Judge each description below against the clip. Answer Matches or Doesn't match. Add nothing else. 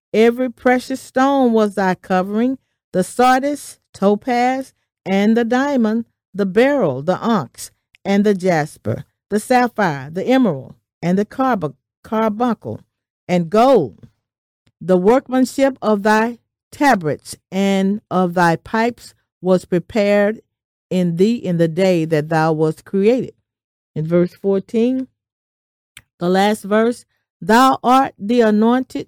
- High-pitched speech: Matches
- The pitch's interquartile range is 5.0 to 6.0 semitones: Matches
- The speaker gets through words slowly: Matches